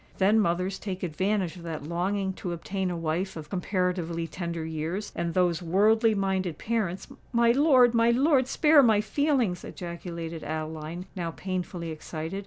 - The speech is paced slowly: No, average, 150 wpm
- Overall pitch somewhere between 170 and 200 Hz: Yes, medium, 185 Hz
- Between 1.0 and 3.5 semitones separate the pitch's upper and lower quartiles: No, average, 3.9 semitones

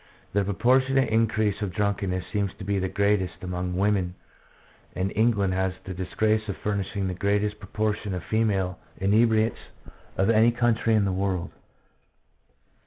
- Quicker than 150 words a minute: No, average, 145 wpm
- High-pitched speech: No, low, 100 Hz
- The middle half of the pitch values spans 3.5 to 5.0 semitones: No, narrow, 2.6 semitones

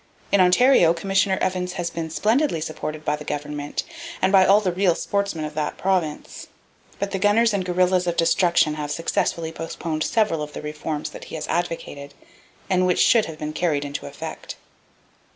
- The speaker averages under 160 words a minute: No, average, 180 wpm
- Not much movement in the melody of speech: No, average, 3.7 semitones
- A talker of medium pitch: Yes, medium, 170 Hz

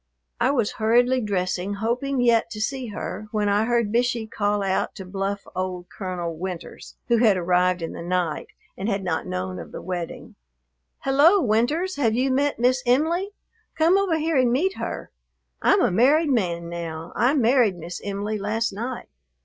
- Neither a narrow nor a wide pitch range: No, wide, 5.8 semitones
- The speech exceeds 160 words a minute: Yes, average, 175 wpm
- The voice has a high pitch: Yes, high, 220 Hz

